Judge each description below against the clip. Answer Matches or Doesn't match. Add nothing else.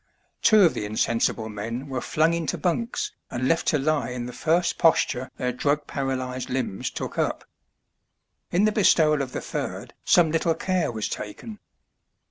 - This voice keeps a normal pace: Matches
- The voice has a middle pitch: Matches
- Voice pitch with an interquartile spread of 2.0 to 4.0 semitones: Doesn't match